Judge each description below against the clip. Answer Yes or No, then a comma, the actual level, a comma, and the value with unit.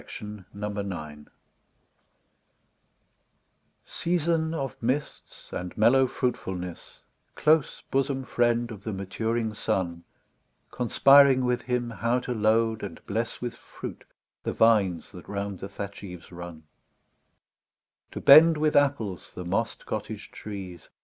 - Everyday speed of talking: No, slow, 115 wpm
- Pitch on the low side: Yes, low, 110 Hz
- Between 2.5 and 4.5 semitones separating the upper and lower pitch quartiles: No, average, 5.0 semitones